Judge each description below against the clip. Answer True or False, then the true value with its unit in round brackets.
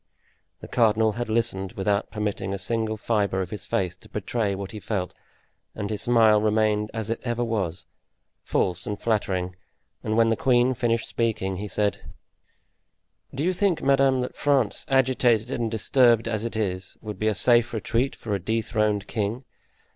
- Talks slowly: False (170 wpm)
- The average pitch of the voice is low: True (110 Hz)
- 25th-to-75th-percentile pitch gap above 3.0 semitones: False (2.7 semitones)